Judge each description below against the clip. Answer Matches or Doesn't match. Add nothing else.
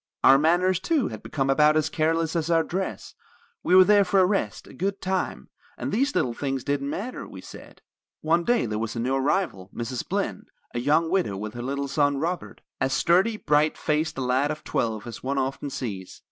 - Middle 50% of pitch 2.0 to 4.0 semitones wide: Doesn't match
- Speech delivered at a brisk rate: Matches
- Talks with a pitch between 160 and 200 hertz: Doesn't match